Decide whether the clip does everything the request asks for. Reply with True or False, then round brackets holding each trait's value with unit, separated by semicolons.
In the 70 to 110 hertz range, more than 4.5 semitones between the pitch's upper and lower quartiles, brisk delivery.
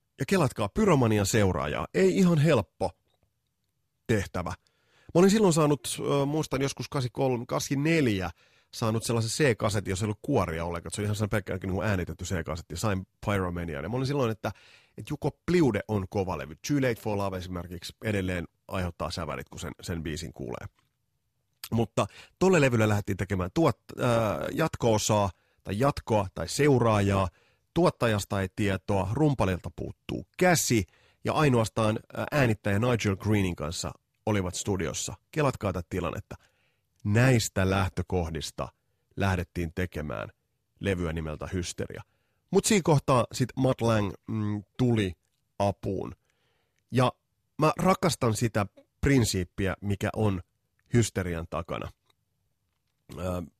False (105 Hz; 5.1 semitones; 125 wpm)